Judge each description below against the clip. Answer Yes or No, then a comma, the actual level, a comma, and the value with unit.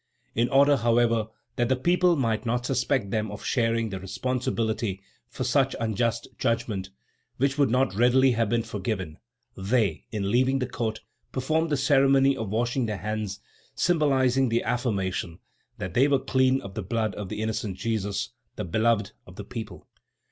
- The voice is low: Yes, low, 115 Hz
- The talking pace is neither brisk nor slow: Yes, average, 165 wpm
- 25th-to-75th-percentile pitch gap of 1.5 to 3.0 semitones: No, average, 3.7 semitones